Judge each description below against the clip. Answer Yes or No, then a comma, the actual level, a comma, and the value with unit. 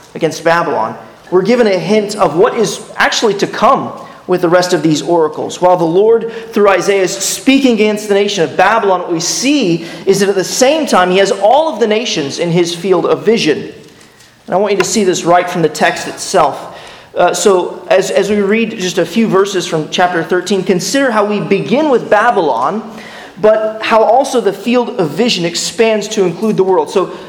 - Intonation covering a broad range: No, average, 3.7 semitones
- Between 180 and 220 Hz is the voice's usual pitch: Yes, high, 190 Hz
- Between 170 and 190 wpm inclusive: No, fast, 205 wpm